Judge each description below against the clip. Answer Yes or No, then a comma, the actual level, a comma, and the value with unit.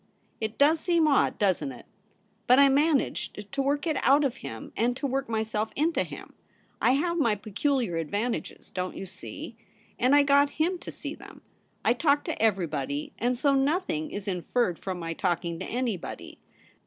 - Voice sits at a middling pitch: No, high, 245 Hz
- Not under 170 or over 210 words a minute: Yes, average, 180 wpm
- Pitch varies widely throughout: Yes, wide, 6.8 semitones